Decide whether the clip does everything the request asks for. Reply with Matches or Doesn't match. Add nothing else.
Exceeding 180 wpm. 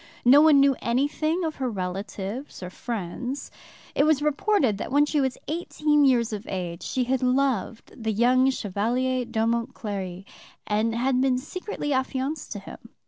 Doesn't match